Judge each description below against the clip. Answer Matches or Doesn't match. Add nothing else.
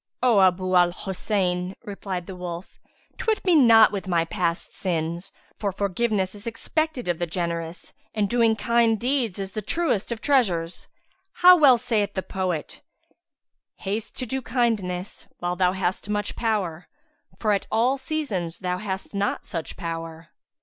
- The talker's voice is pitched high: Matches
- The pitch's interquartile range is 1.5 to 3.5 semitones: Doesn't match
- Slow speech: Doesn't match